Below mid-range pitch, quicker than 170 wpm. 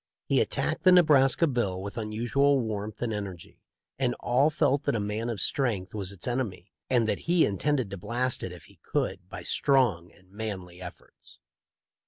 Yes: low, 115 Hz; average, 180 wpm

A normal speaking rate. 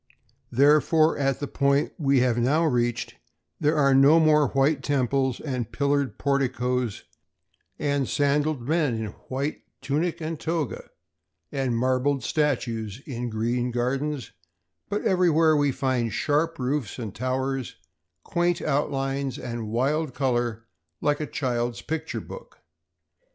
No: slow, 125 wpm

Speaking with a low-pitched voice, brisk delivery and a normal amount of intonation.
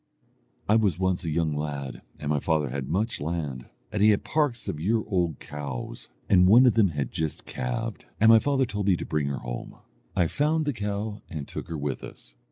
No: very low, 85 Hz; fast, 215 wpm; wide, 6.6 semitones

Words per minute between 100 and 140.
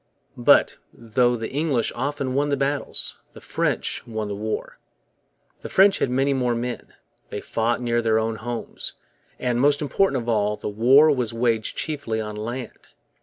No: average, 170 wpm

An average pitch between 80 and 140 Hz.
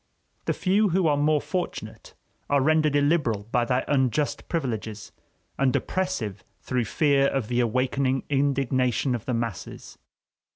Yes: low, 135 Hz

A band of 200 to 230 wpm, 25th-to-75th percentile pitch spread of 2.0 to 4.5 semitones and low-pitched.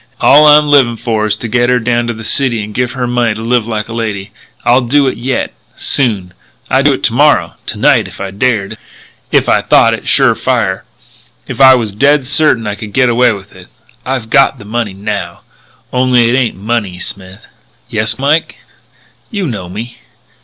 Yes: fast, 205 wpm; average, 3.4 semitones; low, 115 Hz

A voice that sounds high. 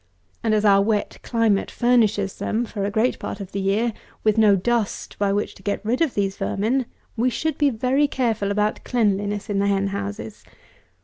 Yes: high, 215 Hz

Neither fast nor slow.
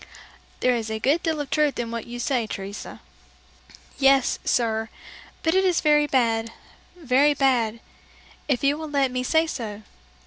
Yes: average, 170 wpm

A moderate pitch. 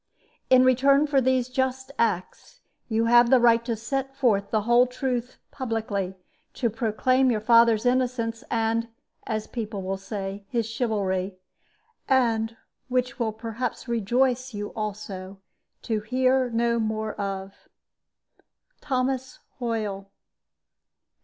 No: high, 230 Hz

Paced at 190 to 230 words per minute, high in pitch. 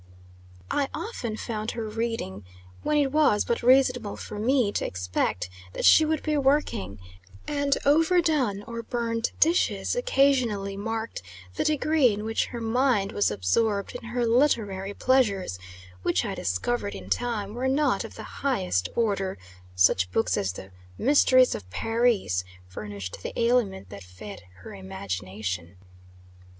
No: average, 140 wpm; high, 220 Hz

